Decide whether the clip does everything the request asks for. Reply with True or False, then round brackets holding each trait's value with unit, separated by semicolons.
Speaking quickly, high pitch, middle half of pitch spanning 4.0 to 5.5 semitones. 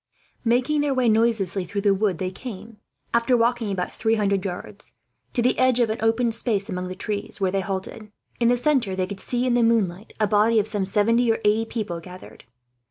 False (215 wpm; 215 Hz; 3.2 semitones)